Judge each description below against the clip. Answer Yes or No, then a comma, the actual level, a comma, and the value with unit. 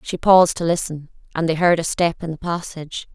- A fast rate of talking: Yes, fast, 230 wpm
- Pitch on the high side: No, medium, 165 Hz